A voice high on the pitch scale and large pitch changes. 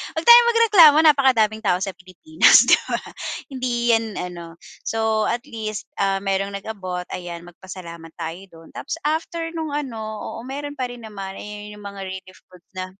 Yes: high, 210 Hz; wide, 6.2 semitones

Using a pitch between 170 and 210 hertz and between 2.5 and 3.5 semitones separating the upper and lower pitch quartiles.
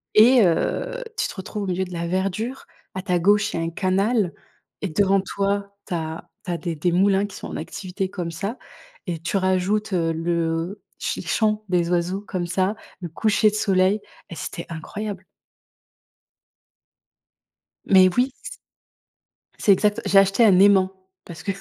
Yes: high, 190 Hz; average, 2.9 semitones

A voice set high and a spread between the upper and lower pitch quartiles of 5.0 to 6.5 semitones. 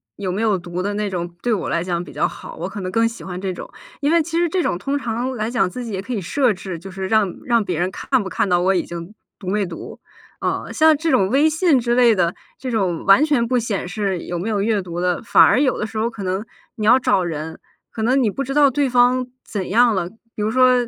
Yes: high, 215 Hz; average, 5.3 semitones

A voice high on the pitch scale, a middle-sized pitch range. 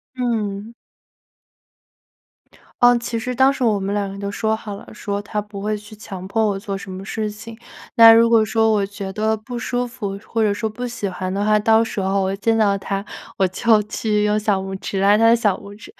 No: high, 210 Hz; narrow, 2.2 semitones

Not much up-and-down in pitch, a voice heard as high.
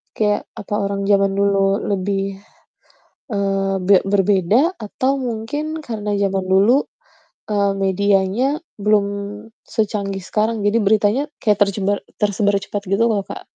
Yes: narrow, 1.7 semitones; high, 200 Hz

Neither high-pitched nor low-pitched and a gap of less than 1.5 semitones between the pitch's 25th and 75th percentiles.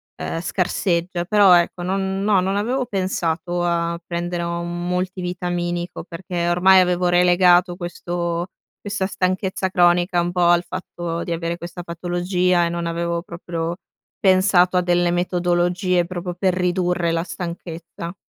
Yes: medium, 175 Hz; narrow, 1.1 semitones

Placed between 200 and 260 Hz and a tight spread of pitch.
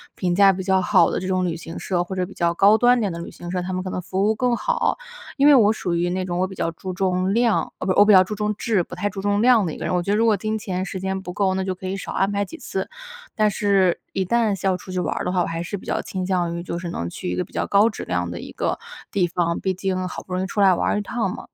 No: high, 190 Hz; narrow, 2.3 semitones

